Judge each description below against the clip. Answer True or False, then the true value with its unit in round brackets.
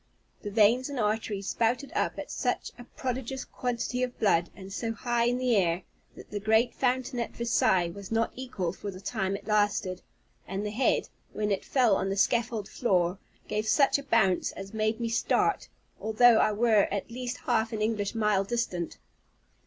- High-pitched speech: True (220 Hz)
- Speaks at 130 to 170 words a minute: False (185 wpm)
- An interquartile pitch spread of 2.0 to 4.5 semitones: True (3.3 semitones)